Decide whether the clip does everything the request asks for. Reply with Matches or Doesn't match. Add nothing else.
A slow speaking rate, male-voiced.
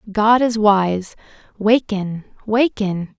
Doesn't match